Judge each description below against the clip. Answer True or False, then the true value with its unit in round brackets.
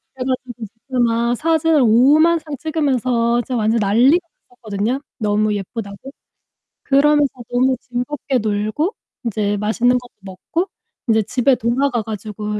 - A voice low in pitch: False (245 Hz)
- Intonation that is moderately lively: True (4.3 semitones)